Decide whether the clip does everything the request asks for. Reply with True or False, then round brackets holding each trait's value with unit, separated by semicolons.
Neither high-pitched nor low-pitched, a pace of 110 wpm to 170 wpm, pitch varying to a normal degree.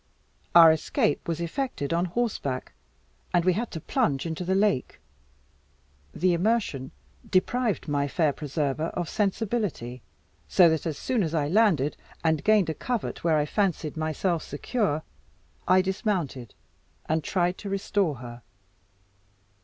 True (170 Hz; 140 wpm; 5.0 semitones)